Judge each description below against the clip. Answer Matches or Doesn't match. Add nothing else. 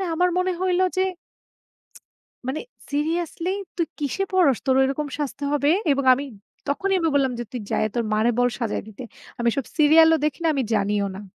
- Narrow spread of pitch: Doesn't match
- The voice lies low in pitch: Doesn't match